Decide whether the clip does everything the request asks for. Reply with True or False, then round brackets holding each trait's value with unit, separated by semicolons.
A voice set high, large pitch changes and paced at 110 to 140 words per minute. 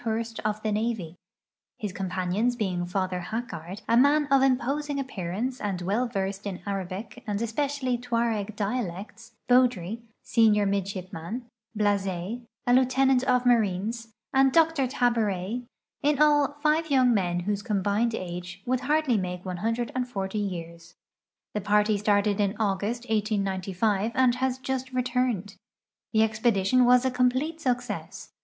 False (220 Hz; 4.3 semitones; 135 wpm)